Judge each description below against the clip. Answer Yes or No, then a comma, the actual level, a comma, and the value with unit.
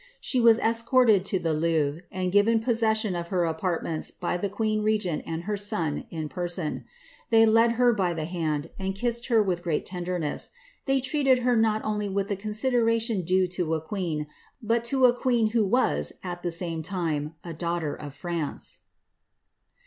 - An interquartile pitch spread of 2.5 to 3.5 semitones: No, average, 5.1 semitones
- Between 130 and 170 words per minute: No, average, 180 wpm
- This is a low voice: No, high, 190 Hz